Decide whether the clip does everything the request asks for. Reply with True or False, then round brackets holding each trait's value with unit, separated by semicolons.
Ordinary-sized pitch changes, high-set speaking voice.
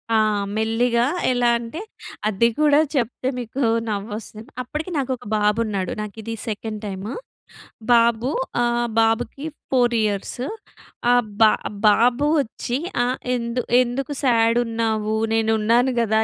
False (2.1 semitones; 230 Hz)